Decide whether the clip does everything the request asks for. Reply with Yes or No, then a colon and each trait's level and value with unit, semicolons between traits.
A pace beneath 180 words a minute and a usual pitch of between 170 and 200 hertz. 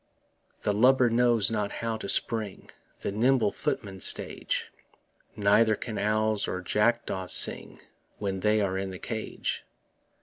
No: slow, 135 wpm; low, 105 Hz